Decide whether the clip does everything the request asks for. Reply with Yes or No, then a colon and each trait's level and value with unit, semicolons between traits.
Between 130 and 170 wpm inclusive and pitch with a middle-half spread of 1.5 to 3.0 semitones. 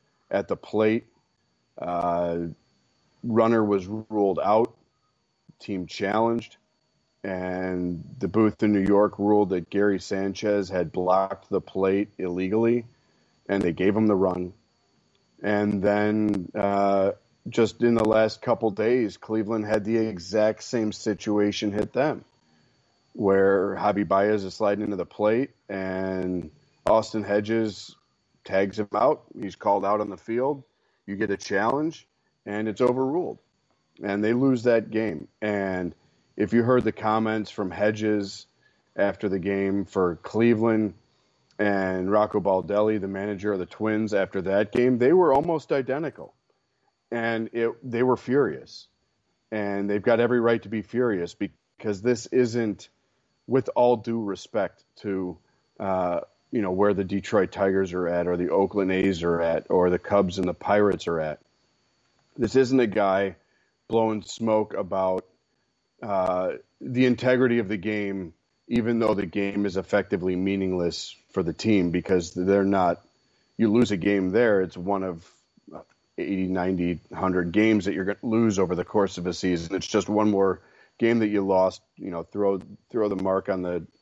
Yes: average, 155 wpm; average, 2.7 semitones